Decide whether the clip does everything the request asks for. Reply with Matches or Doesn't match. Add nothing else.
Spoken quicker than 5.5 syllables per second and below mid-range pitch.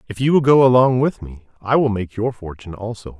Matches